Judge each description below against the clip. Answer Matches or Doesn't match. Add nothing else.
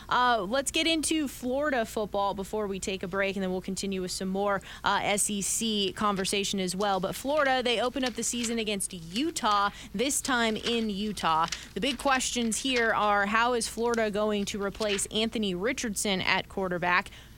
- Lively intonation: Doesn't match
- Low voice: Doesn't match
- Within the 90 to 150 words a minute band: Doesn't match